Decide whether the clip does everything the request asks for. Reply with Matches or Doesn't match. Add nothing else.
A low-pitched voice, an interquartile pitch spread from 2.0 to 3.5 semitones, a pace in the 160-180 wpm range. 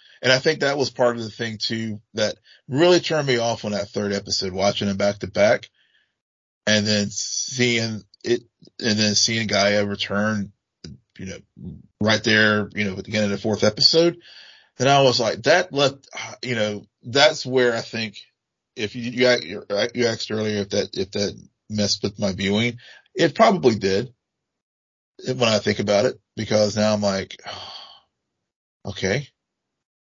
Matches